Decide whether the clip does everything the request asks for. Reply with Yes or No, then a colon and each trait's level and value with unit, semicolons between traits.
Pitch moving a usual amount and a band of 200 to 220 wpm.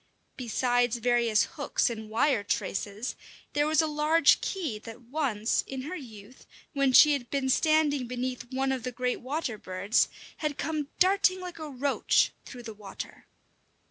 No: average, 4.2 semitones; average, 160 wpm